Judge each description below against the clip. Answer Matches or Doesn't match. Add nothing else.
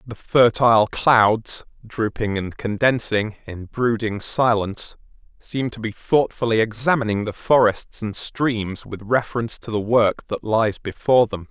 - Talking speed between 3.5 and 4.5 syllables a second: Matches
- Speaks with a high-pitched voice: Doesn't match